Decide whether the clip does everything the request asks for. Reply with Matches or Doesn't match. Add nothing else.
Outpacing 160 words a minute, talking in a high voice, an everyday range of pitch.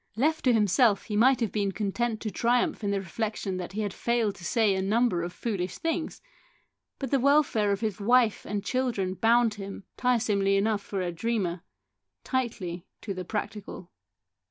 Matches